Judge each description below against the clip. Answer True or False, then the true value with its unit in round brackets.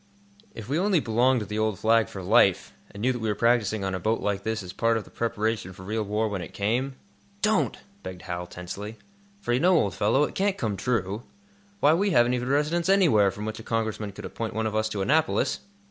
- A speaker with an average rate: False (240 wpm)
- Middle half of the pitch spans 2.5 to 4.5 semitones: True (3.6 semitones)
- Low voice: True (110 Hz)